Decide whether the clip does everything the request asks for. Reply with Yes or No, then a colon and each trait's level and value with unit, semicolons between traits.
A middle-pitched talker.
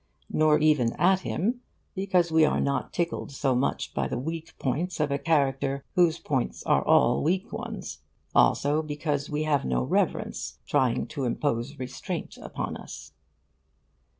Yes: medium, 150 Hz